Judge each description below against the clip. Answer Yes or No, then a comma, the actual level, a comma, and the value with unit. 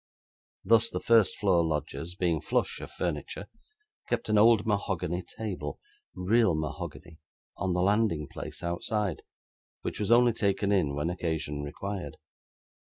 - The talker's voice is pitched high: No, very low, 95 Hz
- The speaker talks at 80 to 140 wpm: Yes, slow, 135 wpm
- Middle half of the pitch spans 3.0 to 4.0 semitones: No, average, 4.4 semitones